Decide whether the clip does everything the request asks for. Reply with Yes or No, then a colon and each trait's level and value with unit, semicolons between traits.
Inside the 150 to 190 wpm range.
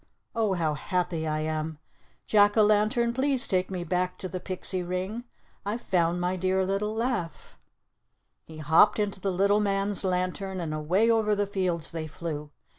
Yes: average, 170 wpm